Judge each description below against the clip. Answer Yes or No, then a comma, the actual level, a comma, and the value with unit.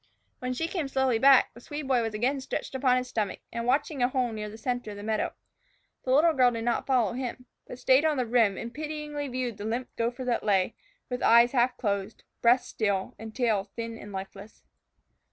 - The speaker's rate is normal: No, fast, 215 wpm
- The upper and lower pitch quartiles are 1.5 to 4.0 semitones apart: Yes, average, 2.9 semitones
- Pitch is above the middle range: Yes, high, 245 Hz